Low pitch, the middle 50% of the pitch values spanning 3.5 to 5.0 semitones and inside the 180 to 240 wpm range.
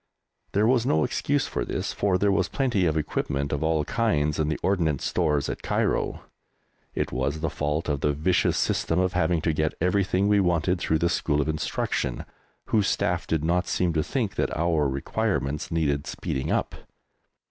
Yes: very low, 80 Hz; average, 3.9 semitones; average, 185 wpm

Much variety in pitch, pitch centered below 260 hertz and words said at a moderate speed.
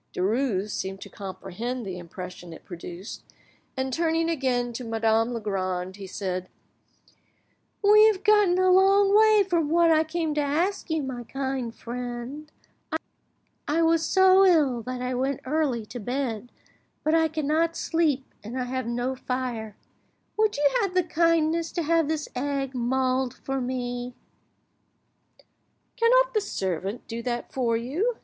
No: wide, 5.9 semitones; very high, 265 Hz; average, 150 wpm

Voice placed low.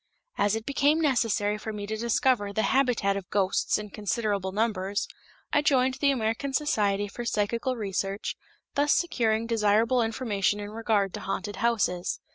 No: high, 220 Hz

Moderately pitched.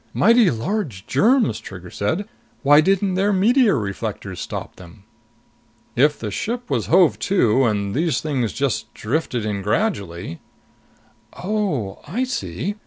Yes: medium, 145 Hz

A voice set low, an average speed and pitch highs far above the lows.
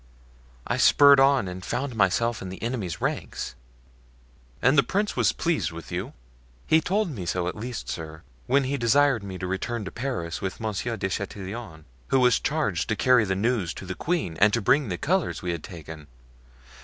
Yes: low, 110 Hz; average, 190 wpm; wide, 6.5 semitones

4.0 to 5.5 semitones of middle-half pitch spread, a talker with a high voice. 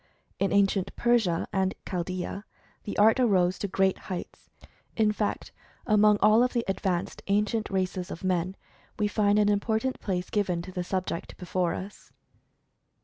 No: narrow, 2.5 semitones; high, 195 Hz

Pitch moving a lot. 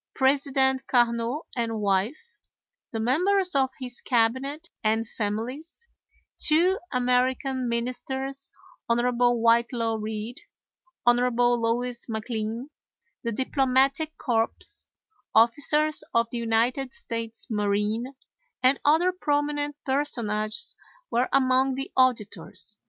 No: average, 3.1 semitones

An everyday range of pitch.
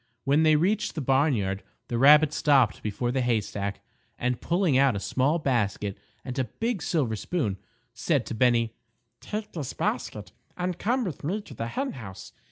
No: wide, 6.0 semitones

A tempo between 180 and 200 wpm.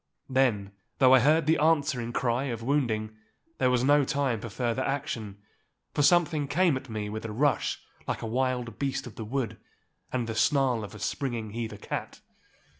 Yes: average, 185 wpm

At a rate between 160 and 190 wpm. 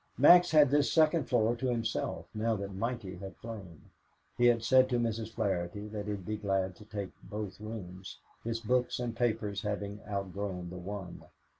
Yes: average, 175 wpm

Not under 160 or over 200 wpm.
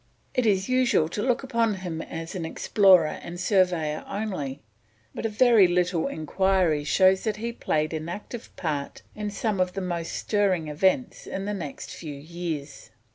Yes: average, 165 wpm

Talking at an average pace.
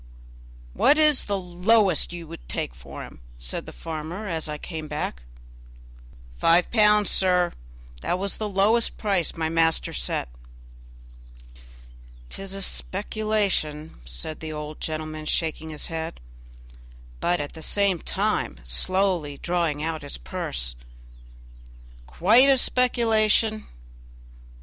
No: slow, 120 wpm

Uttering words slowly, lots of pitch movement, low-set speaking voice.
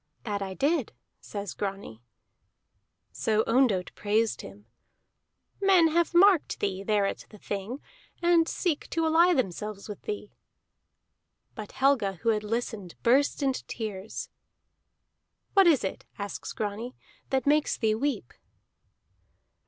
No: slow, 125 wpm; wide, 6.3 semitones; high, 225 Hz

